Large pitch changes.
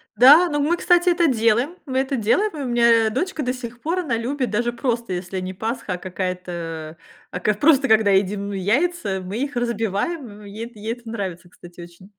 Yes: wide, 5.9 semitones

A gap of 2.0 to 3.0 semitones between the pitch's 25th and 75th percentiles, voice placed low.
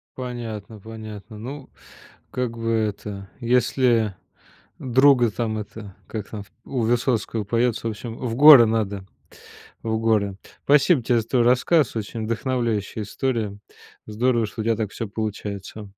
Yes: narrow, 2.5 semitones; low, 115 Hz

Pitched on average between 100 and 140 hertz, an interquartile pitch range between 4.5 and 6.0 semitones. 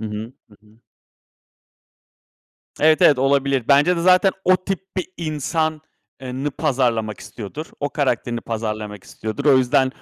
Yes: low, 135 Hz; average, 5.3 semitones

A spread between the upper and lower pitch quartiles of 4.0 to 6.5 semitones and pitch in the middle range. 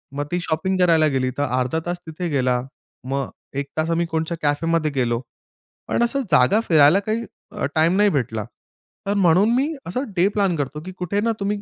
Yes: average, 4.9 semitones; medium, 160 Hz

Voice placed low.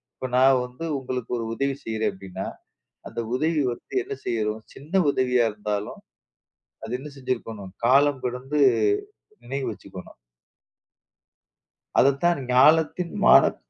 Yes: low, 130 Hz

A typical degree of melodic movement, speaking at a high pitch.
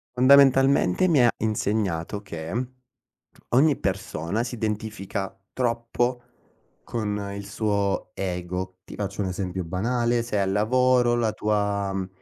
No: average, 3.8 semitones; low, 105 Hz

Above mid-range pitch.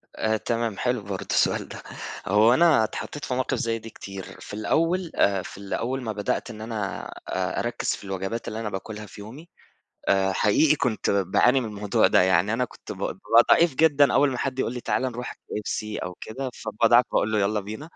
No: low, 110 Hz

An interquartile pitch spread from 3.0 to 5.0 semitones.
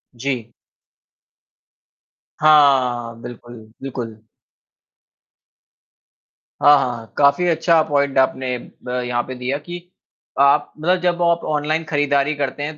Yes: average, 3.4 semitones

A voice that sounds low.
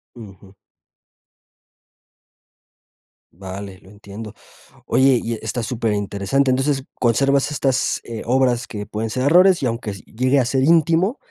Yes: low, 120 Hz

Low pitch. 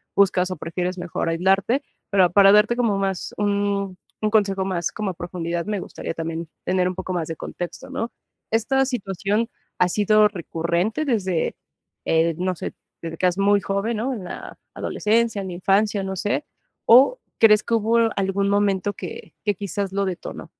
No: high, 195 Hz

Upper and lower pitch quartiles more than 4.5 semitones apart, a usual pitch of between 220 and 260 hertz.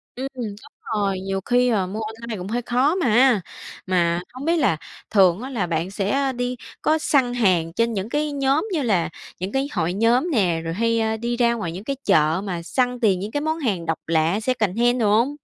Yes: average, 5.1 semitones; high, 225 Hz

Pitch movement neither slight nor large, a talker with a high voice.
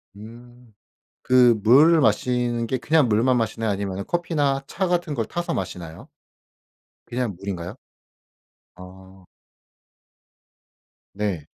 No: average, 4.8 semitones; low, 115 Hz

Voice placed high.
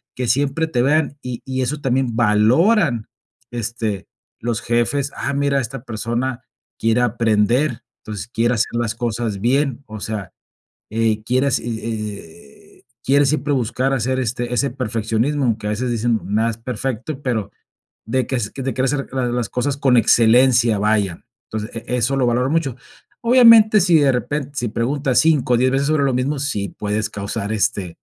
No: low, 120 Hz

